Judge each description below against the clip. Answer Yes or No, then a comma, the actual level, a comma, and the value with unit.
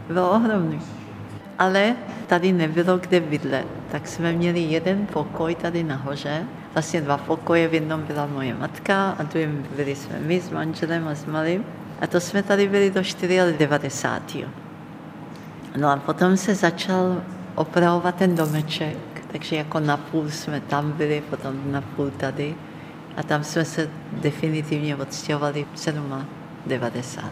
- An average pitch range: Yes, average, 3.0 semitones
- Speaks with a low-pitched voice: No, medium, 160 Hz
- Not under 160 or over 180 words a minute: No, average, 145 wpm